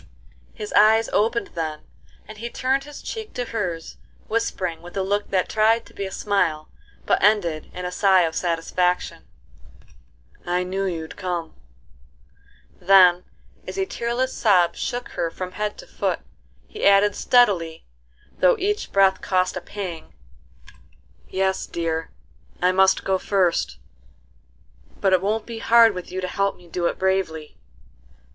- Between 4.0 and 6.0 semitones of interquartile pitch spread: No, average, 3.4 semitones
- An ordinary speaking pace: Yes, average, 150 wpm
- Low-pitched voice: No, high, 190 Hz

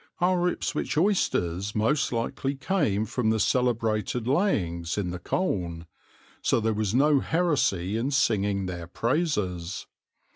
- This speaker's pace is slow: Yes, slow, 130 wpm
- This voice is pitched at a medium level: No, low, 115 Hz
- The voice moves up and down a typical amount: No, wide, 7.0 semitones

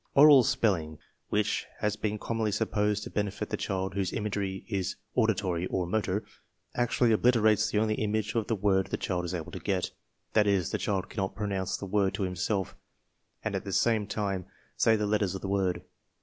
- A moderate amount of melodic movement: No, narrow, 2.2 semitones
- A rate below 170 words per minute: No, average, 190 wpm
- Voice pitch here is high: No, low, 100 Hz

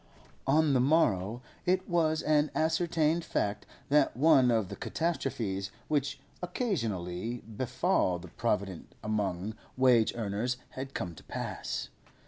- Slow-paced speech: Yes, slow, 120 wpm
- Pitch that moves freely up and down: Yes, wide, 7.3 semitones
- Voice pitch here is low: Yes, low, 125 Hz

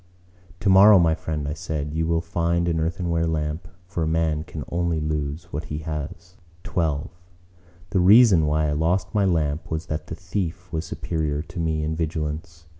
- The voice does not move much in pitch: Yes, narrow, 2.0 semitones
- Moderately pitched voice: No, very low, 80 Hz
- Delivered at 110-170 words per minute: No, average, 180 wpm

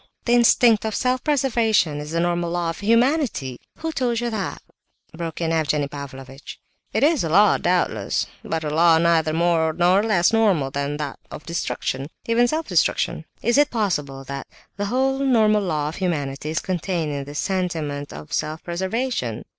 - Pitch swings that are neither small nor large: No, wide, 7.0 semitones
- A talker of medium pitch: Yes, medium, 175 Hz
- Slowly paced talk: No, average, 175 wpm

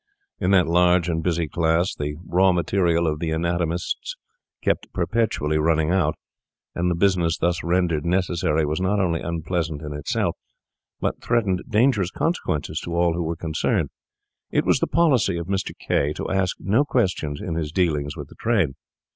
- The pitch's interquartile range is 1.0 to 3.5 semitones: Yes, average, 2.7 semitones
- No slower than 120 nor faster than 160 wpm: No, average, 170 wpm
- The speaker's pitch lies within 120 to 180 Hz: No, very low, 85 Hz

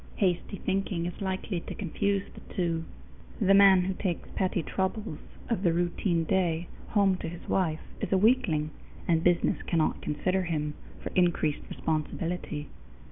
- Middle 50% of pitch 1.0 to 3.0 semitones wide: Yes, average, 2.7 semitones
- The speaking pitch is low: No, medium, 180 Hz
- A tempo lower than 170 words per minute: Yes, average, 150 wpm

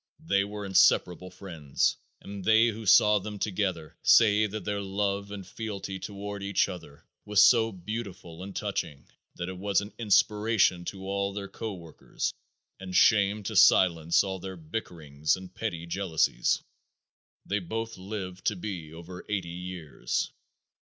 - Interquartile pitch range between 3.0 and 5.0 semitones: No, narrow, 2.5 semitones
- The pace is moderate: Yes, average, 150 wpm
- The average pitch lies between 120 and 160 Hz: No, low, 100 Hz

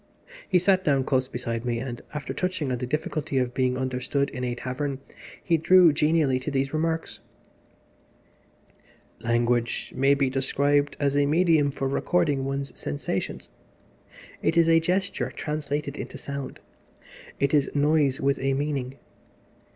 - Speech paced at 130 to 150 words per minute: Yes, average, 145 wpm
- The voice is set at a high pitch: No, medium, 140 Hz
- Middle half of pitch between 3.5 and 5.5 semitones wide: No, average, 2.8 semitones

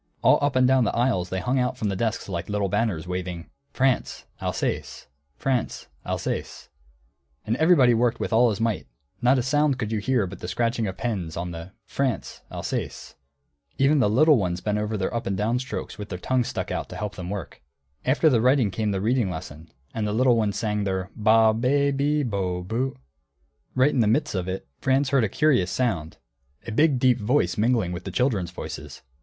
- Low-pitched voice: Yes, low, 110 Hz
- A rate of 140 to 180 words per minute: No, fast, 205 wpm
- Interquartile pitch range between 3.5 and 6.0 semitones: Yes, average, 5.2 semitones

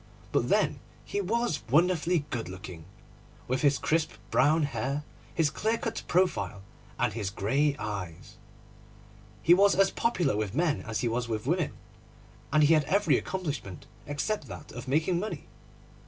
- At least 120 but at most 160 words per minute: Yes, average, 155 wpm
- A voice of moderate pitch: Yes, medium, 145 Hz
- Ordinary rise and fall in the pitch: No, wide, 7.6 semitones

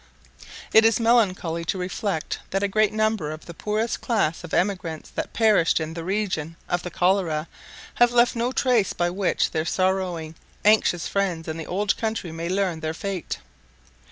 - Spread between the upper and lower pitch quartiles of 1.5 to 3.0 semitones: No, average, 4.4 semitones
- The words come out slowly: No, average, 175 wpm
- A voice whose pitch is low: No, medium, 185 Hz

